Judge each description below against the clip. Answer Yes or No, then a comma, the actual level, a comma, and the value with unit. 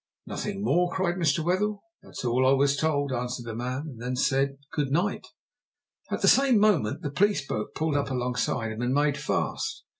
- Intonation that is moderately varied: No, wide, 5.8 semitones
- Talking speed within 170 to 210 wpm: Yes, average, 190 wpm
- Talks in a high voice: No, medium, 140 Hz